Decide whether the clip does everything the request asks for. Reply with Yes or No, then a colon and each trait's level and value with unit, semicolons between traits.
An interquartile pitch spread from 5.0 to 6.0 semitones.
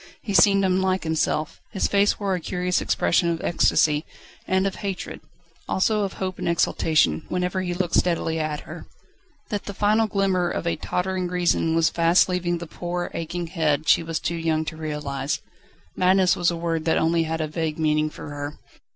No: narrow, 2.6 semitones